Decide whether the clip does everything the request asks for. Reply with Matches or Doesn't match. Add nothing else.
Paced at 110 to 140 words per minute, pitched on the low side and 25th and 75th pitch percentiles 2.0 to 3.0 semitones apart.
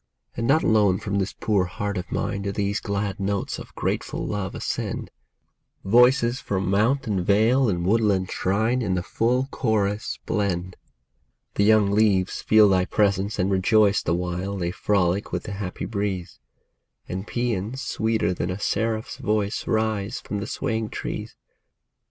Doesn't match